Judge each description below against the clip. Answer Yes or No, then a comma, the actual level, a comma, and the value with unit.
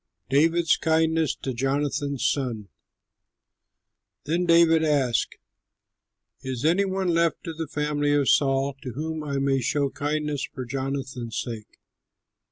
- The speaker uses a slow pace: Yes, slow, 125 wpm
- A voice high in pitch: No, medium, 145 Hz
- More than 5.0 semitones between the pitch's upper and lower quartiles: No, average, 3.0 semitones